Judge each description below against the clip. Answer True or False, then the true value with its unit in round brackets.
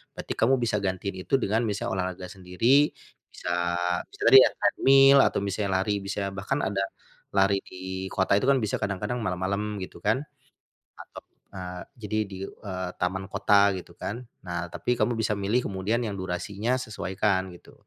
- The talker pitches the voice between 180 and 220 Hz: False (100 Hz)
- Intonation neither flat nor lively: True (3.0 semitones)